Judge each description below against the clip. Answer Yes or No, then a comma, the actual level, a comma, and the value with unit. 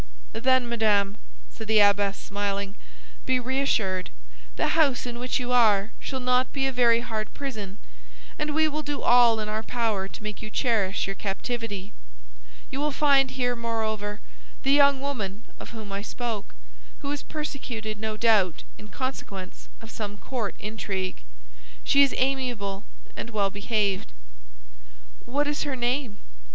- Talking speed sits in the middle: Yes, average, 155 wpm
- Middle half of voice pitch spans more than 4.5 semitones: No, average, 4.2 semitones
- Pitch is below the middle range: No, high, 230 Hz